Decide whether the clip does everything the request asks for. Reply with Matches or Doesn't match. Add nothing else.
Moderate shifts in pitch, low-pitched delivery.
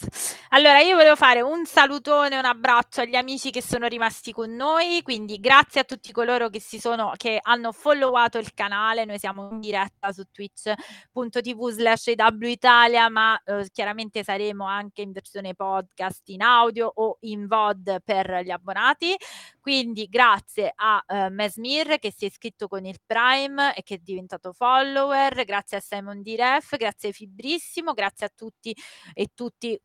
Doesn't match